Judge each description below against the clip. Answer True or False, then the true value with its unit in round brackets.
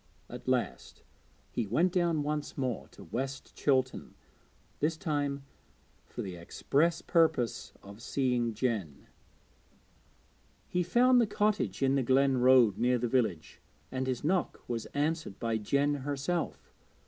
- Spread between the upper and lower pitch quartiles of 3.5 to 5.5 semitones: True (4.7 semitones)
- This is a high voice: False (135 Hz)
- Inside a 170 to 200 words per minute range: False (135 wpm)